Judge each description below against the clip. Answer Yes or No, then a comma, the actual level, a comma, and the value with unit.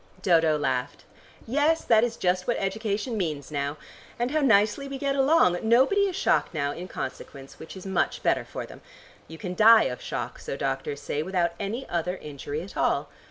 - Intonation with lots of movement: Yes, wide, 7.0 semitones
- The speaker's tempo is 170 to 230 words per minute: Yes, average, 190 wpm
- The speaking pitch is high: Yes, high, 195 Hz